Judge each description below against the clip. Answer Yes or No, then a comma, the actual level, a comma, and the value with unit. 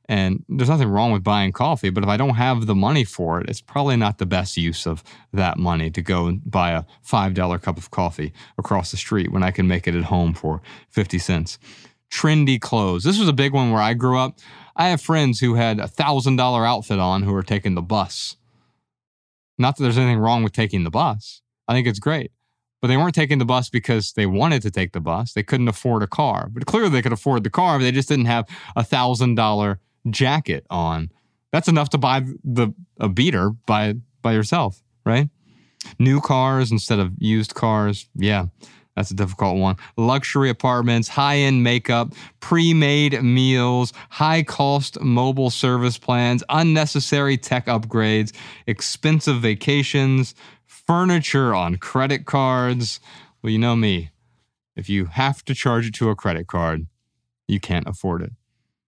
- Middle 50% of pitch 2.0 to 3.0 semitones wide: No, average, 5.0 semitones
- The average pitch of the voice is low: Yes, low, 120 Hz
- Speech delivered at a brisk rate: No, average, 185 wpm